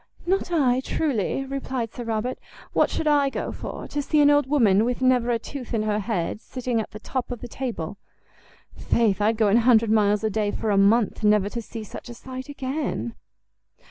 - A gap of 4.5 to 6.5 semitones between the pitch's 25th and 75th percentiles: No, average, 3.7 semitones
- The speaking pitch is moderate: No, high, 235 Hz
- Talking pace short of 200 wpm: No, fast, 205 wpm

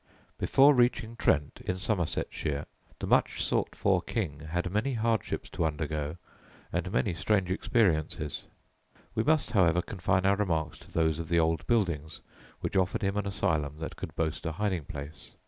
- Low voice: Yes, very low, 90 Hz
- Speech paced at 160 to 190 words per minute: Yes, average, 165 wpm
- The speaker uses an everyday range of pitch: Yes, average, 4.7 semitones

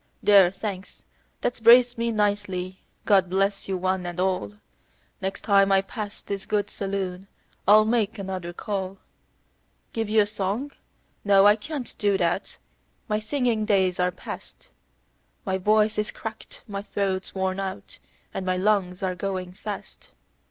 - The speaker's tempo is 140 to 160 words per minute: Yes, average, 150 wpm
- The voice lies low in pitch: No, high, 195 Hz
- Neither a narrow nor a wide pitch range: No, narrow, 2.2 semitones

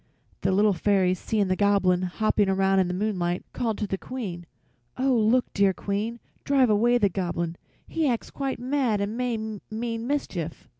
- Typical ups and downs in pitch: Yes, average, 3.9 semitones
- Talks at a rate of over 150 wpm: Yes, average, 170 wpm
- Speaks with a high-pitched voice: Yes, high, 210 Hz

